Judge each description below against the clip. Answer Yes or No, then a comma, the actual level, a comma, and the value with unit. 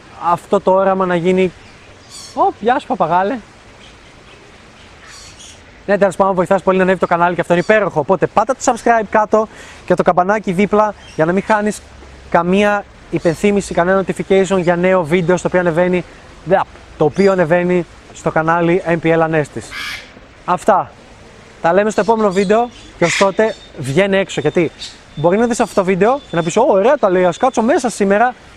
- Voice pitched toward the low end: No, high, 190 Hz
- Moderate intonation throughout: Yes, average, 3.1 semitones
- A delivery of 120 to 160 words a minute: No, fast, 170 wpm